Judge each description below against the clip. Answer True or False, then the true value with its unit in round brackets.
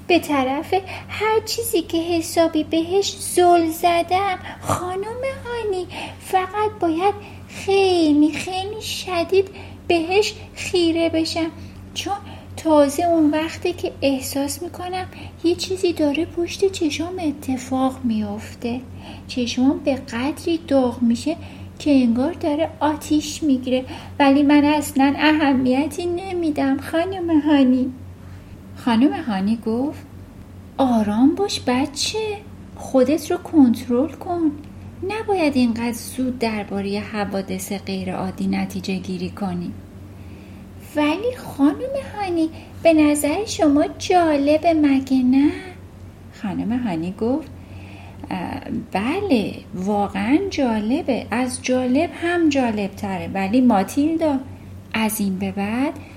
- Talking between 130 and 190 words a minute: False (105 wpm)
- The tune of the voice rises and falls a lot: True (6.3 semitones)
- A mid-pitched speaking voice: False (290 Hz)